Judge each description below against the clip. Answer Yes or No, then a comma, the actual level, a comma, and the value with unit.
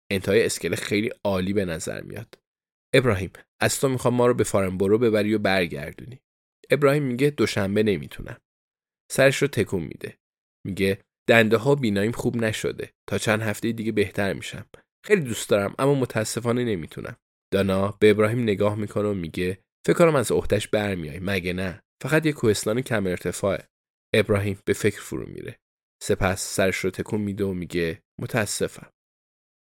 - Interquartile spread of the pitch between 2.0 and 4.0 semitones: Yes, average, 3.1 semitones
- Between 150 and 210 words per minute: Yes, fast, 155 wpm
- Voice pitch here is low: Yes, low, 105 Hz